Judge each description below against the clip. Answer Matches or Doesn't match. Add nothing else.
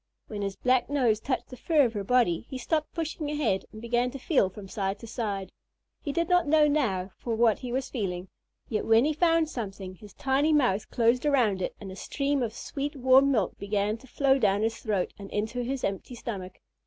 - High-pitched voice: Matches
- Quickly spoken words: Matches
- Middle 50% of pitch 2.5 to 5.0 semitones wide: Doesn't match